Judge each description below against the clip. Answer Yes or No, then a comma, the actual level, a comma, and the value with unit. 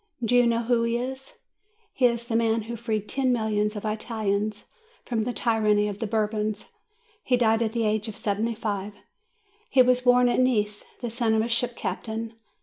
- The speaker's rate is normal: Yes, average, 195 wpm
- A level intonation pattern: Yes, narrow, 2.1 semitones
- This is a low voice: No, high, 225 Hz